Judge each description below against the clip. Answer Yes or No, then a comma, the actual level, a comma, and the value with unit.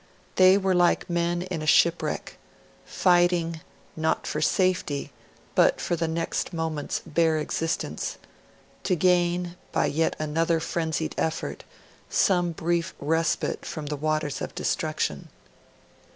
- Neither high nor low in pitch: Yes, medium, 165 Hz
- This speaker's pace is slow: Yes, slow, 125 wpm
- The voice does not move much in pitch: Yes, narrow, 1.9 semitones